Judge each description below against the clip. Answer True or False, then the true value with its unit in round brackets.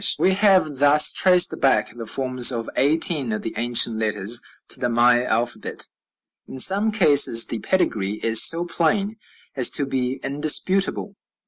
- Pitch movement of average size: False (6.7 semitones)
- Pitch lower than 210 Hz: True (135 Hz)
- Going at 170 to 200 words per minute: False (150 wpm)